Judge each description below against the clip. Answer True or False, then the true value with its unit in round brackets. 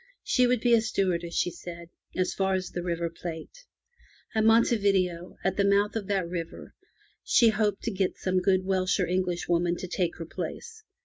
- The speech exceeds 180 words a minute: True (195 wpm)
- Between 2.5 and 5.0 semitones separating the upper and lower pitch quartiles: True (2.9 semitones)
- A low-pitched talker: False (185 Hz)